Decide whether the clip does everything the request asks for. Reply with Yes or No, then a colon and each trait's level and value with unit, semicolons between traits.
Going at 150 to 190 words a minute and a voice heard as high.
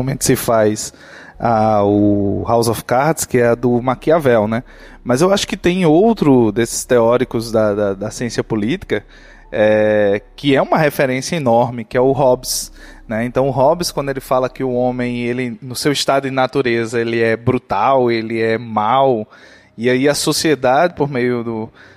No: average, 180 wpm; low, 125 Hz